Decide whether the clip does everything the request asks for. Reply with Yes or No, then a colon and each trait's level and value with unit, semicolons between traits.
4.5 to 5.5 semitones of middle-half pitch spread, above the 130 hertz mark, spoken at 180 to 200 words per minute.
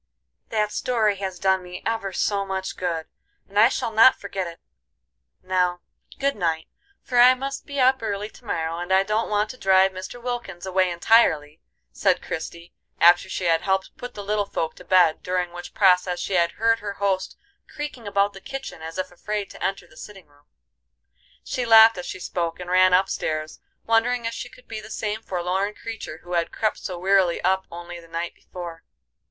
No: average, 3.7 semitones; high, 190 Hz; average, 195 wpm